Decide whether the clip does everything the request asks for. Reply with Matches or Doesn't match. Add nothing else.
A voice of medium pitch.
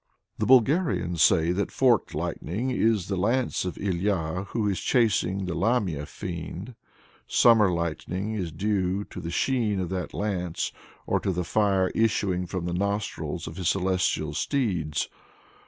Doesn't match